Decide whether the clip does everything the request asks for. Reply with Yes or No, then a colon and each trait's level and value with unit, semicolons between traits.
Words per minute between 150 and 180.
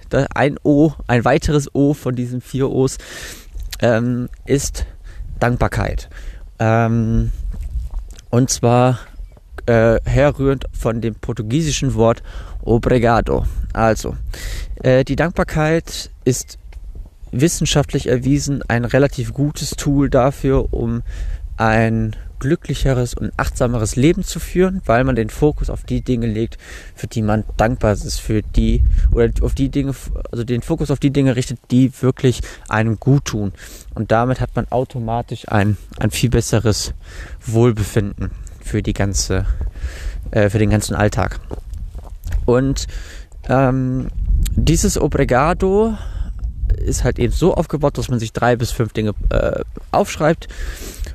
No: average, 130 wpm